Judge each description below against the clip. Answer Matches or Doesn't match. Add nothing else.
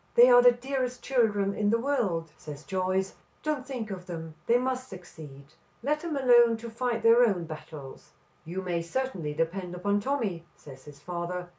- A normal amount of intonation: Doesn't match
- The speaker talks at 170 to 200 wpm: Matches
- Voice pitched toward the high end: Matches